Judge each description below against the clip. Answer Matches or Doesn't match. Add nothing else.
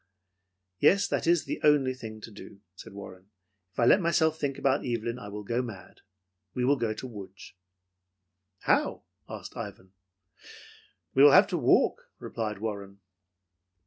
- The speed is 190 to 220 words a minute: Doesn't match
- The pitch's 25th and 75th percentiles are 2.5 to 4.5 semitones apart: Doesn't match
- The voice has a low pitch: Matches